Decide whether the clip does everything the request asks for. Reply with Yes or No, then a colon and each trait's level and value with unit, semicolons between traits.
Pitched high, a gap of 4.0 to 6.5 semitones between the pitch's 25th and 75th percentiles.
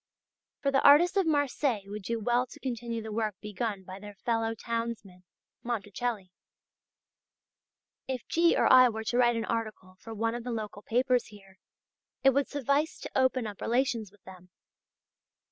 No: high, 230 Hz; average, 3.4 semitones